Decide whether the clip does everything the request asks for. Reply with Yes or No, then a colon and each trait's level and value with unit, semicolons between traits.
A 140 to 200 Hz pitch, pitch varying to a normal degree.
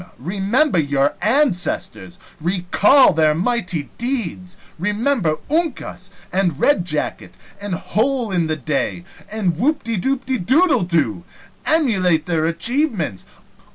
No: high, 190 Hz; wide, 7.4 semitones